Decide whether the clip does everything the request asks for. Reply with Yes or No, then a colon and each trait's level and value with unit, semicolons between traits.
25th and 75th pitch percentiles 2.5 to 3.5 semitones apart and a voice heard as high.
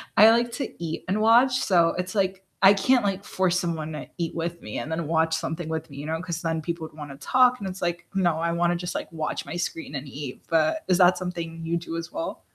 No: average, 2.8 semitones; medium, 170 Hz